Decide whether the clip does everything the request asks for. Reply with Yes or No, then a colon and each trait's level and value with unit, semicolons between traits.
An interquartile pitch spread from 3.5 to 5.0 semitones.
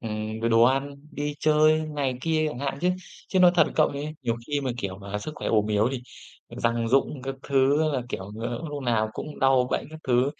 Yes: average, 4.3 semitones